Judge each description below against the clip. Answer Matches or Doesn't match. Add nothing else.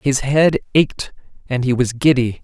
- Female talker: Doesn't match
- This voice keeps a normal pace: Matches